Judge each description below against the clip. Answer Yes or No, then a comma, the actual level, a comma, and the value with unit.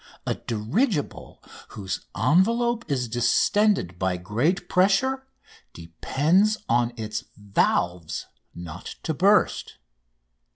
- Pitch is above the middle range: No, low, 130 Hz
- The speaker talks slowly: Yes, slow, 90 wpm